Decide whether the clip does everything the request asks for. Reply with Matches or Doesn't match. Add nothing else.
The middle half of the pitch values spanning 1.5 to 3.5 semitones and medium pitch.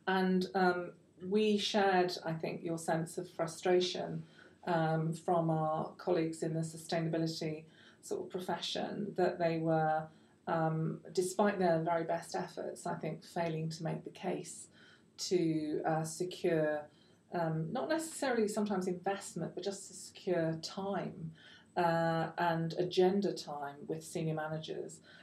Matches